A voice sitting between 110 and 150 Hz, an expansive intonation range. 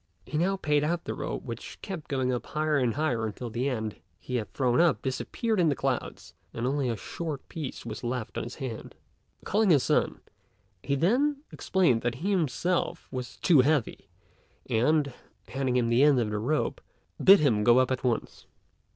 No: low, 135 Hz; average, 4.6 semitones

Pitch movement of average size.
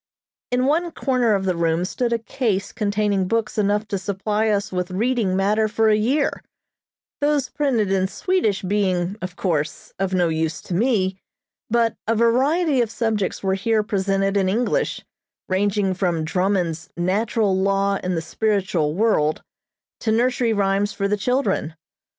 Yes: average, 3.4 semitones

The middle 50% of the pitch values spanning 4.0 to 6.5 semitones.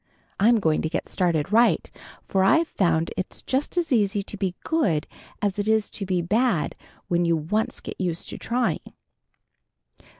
Yes: average, 4.6 semitones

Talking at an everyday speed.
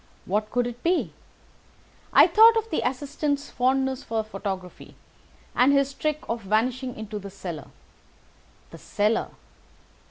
No: slow, 130 wpm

